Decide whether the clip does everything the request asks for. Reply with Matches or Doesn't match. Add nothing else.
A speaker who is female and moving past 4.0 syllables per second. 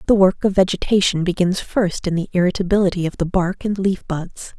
Matches